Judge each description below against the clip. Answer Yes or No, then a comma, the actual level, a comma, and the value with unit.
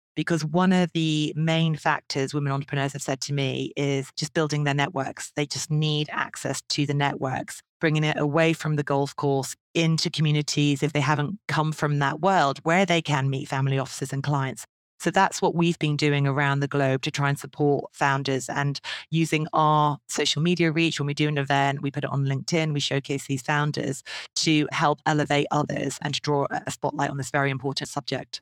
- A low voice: No, medium, 145 Hz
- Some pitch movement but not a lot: No, narrow, 1.8 semitones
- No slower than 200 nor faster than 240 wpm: Yes, fast, 205 wpm